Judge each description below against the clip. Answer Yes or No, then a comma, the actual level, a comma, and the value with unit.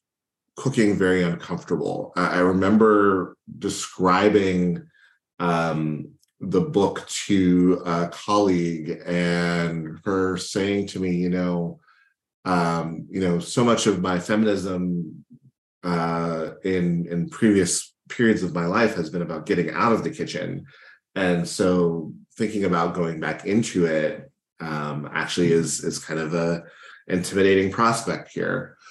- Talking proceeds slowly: Yes, slow, 125 wpm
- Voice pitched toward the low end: Yes, very low, 90 Hz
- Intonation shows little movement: Yes, narrow, 2.3 semitones